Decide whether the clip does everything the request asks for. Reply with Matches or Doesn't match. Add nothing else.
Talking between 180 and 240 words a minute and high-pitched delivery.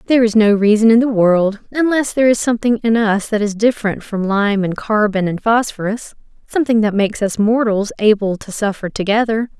Matches